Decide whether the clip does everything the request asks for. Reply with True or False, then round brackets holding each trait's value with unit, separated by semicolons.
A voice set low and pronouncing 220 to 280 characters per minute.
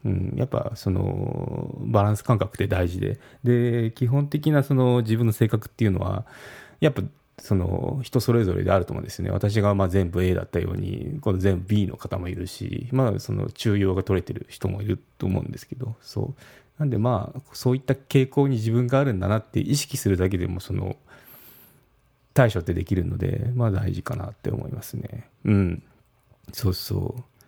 False (115 Hz; 360 characters per minute)